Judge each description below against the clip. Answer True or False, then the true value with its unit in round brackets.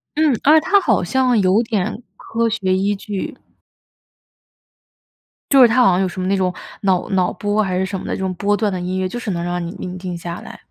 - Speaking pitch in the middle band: False (195 Hz)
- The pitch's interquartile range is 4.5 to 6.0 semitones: False (3.7 semitones)